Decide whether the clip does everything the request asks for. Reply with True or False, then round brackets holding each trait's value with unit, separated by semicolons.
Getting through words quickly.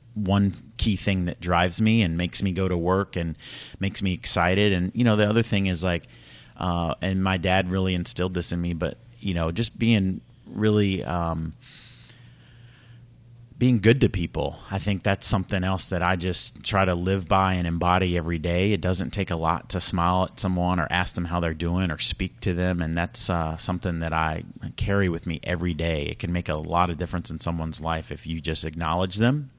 True (215 wpm)